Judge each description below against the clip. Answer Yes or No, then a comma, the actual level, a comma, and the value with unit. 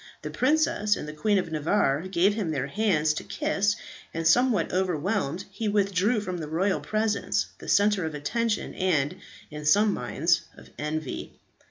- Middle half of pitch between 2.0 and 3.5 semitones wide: No, average, 5.2 semitones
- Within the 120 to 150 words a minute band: No, average, 165 wpm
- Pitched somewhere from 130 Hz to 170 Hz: No, medium, 185 Hz